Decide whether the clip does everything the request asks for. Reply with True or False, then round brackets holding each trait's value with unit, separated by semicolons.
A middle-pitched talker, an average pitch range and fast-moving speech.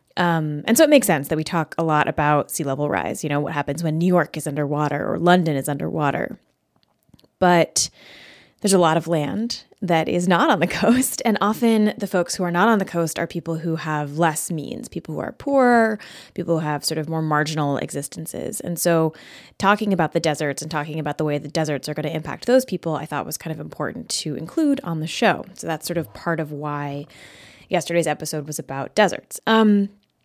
True (165 Hz; 3.3 semitones; 220 wpm)